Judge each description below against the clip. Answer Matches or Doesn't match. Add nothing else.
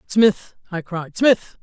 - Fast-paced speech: Doesn't match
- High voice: Matches